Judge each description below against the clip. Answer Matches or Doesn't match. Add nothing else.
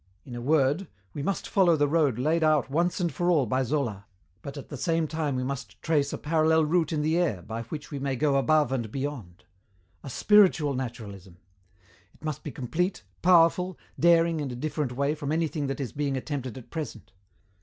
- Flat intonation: Doesn't match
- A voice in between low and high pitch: Matches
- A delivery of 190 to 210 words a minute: Matches